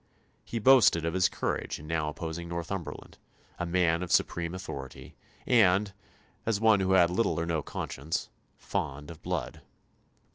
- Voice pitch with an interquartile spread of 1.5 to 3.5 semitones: Yes, average, 2.7 semitones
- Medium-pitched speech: No, very low, 85 Hz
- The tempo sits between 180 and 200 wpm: No, average, 150 wpm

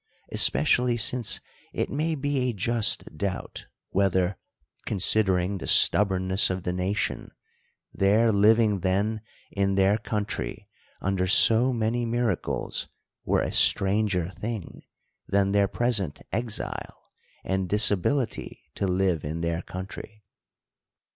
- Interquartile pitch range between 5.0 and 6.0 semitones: No, average, 3.2 semitones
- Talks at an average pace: No, slow, 115 wpm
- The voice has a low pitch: Yes, low, 100 Hz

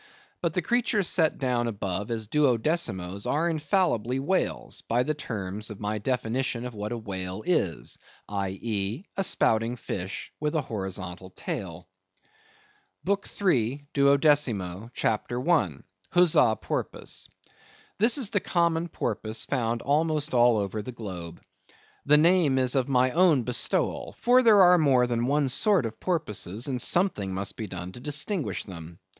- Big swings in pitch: Yes, wide, 6.8 semitones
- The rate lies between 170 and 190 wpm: No, average, 145 wpm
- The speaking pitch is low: Yes, low, 125 Hz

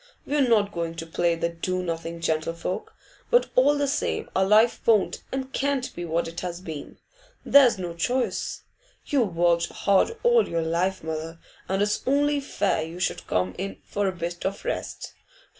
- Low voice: No, medium, 185 Hz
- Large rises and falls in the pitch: Yes, wide, 6.6 semitones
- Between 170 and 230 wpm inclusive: Yes, average, 175 wpm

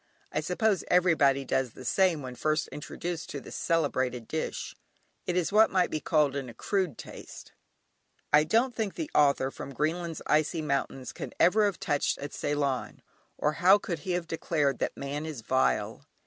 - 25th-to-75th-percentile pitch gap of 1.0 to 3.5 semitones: No, average, 4.3 semitones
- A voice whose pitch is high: No, medium, 155 Hz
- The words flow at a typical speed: Yes, average, 175 wpm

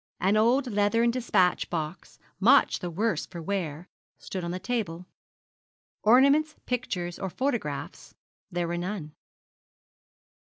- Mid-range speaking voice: No, high, 195 Hz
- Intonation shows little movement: No, wide, 5.4 semitones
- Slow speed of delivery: Yes, slow, 120 wpm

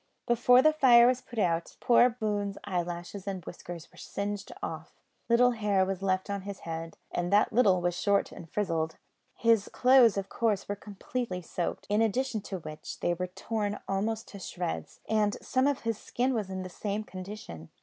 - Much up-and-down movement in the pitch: No, average, 3.8 semitones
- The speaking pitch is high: Yes, high, 200 Hz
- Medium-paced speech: Yes, average, 185 wpm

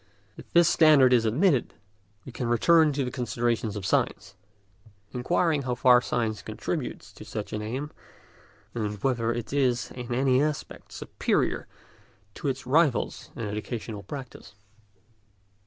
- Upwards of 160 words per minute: No, average, 140 wpm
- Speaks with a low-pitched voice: Yes, low, 125 Hz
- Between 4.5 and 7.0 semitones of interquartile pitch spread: No, average, 3.4 semitones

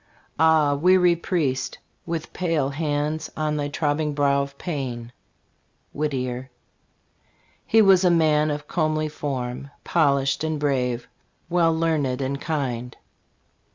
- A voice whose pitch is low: No, medium, 150 Hz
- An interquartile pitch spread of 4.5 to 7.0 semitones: No, average, 2.7 semitones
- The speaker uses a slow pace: Yes, slow, 120 wpm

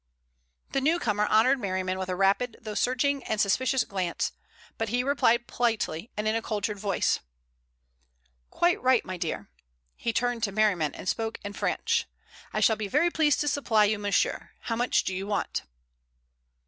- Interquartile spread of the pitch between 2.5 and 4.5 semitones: Yes, average, 3.8 semitones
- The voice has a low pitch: No, high, 220 Hz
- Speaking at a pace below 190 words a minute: Yes, average, 170 wpm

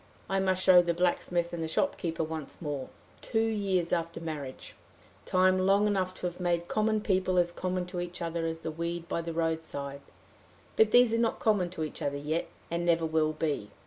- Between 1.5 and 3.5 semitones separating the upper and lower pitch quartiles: Yes, narrow, 2.4 semitones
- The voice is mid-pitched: Yes, medium, 175 Hz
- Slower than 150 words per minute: No, average, 200 wpm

